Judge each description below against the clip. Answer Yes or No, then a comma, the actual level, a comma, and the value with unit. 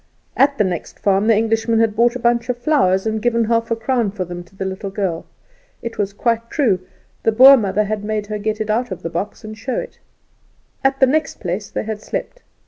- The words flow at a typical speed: No, fast, 225 wpm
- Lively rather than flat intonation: No, average, 2.9 semitones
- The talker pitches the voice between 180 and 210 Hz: No, high, 220 Hz